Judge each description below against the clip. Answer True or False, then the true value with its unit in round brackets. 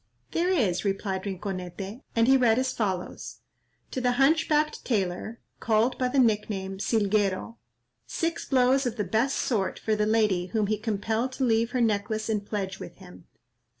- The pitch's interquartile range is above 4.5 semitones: False (4.2 semitones)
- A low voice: False (220 Hz)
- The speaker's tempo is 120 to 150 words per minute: False (175 wpm)